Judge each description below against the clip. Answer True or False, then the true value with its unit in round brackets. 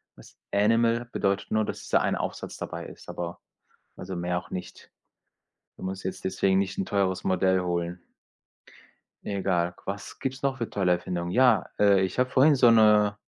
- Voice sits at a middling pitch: False (95 Hz)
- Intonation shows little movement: False (3.1 semitones)